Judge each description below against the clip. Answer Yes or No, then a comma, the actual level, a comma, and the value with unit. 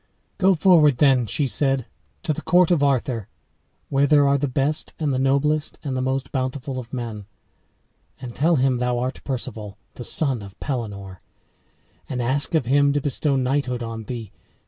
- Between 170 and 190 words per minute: Yes, average, 175 wpm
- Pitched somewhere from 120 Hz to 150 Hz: Yes, low, 135 Hz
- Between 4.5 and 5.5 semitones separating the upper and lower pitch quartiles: No, average, 2.8 semitones